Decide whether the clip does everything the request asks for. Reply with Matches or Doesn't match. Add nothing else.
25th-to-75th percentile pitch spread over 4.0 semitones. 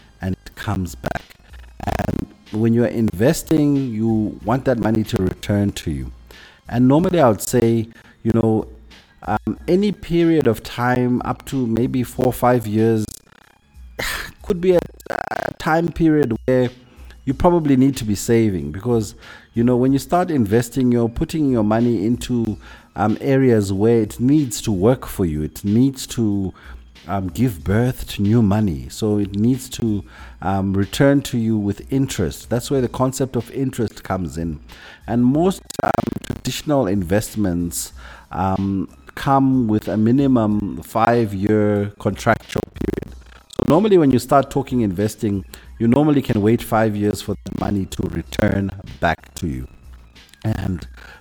Matches